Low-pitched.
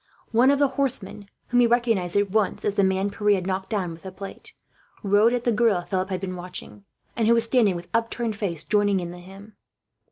No: high, 205 Hz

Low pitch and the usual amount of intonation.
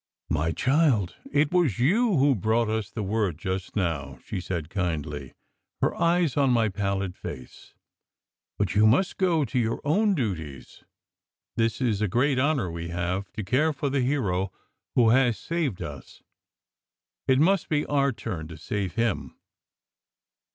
No: low, 110 Hz; wide, 7.4 semitones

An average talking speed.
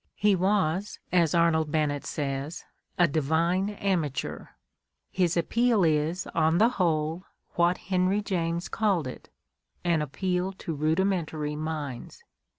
No: slow, 120 wpm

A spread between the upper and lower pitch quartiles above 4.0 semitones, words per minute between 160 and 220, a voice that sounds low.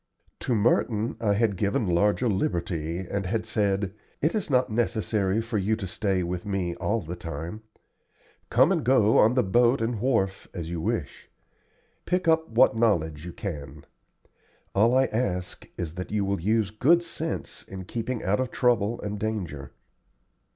Yes: average, 4.4 semitones; average, 165 wpm; low, 105 Hz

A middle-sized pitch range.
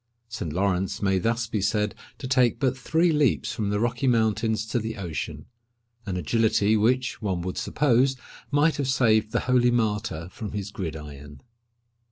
Yes: average, 3.5 semitones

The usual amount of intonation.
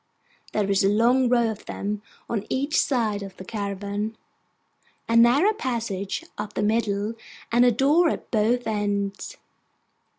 Yes: average, 3.1 semitones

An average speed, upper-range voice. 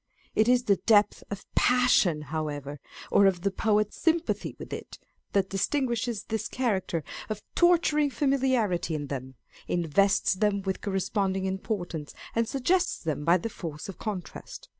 Yes: average, 150 wpm; high, 200 Hz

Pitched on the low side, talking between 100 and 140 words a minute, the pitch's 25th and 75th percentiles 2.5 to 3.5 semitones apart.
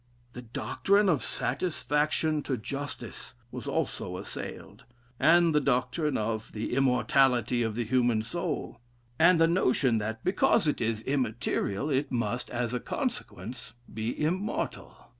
No: low, 130 Hz; slow, 135 wpm; average, 4.6 semitones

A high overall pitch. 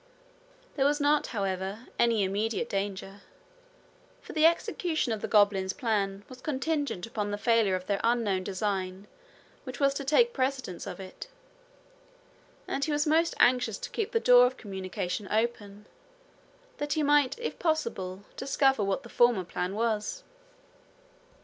Yes: high, 230 Hz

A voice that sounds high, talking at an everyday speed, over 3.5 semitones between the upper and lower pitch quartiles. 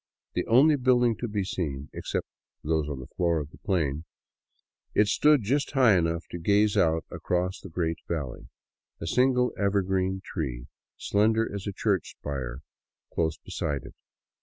No: very low, 95 Hz; average, 160 wpm; average, 5.3 semitones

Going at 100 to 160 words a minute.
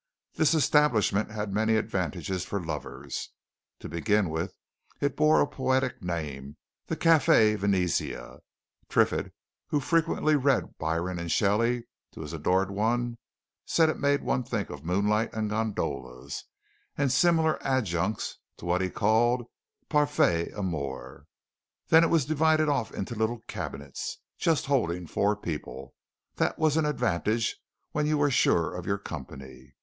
Yes: average, 140 wpm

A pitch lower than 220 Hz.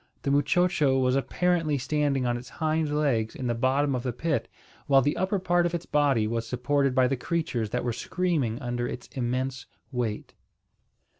Yes: low, 135 Hz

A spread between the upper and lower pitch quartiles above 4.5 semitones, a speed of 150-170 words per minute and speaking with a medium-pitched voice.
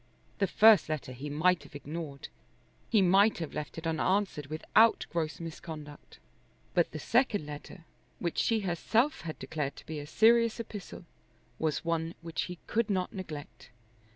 Yes: average, 5.0 semitones; average, 155 wpm; medium, 165 Hz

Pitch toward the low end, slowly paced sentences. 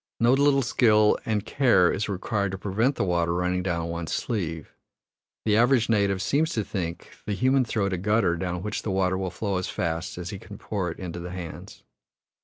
No: very low, 95 Hz; fast, 205 wpm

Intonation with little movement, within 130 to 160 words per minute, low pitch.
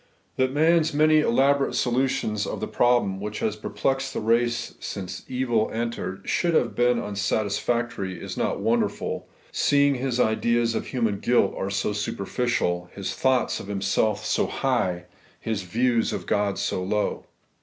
No: average, 4.2 semitones; average, 150 wpm; low, 115 Hz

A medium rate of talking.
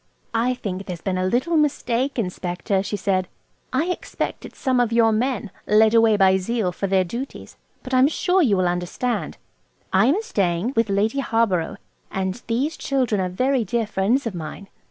Yes: average, 175 wpm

